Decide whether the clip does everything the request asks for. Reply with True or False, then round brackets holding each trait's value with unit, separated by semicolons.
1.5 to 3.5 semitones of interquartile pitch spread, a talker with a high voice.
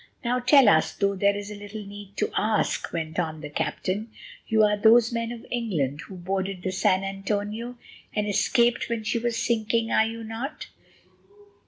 True (2.8 semitones; 210 Hz)